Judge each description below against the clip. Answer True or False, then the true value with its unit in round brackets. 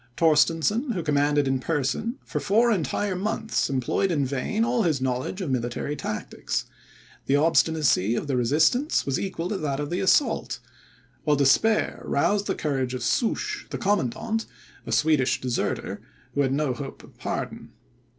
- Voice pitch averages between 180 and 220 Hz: False (150 Hz)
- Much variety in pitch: True (7.2 semitones)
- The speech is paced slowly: False (160 wpm)